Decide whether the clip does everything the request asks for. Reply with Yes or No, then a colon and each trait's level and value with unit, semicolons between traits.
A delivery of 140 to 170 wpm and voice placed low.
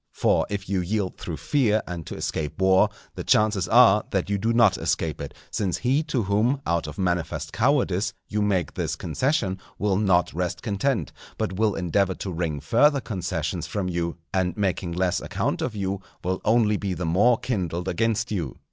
No: average, 185 wpm; very low, 95 Hz